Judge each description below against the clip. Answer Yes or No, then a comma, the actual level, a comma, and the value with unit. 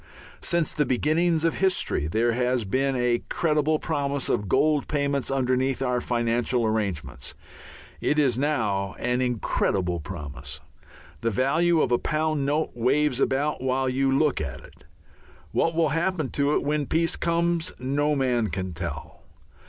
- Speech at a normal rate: Yes, average, 150 wpm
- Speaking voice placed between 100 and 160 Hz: Yes, low, 135 Hz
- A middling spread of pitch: Yes, average, 4.3 semitones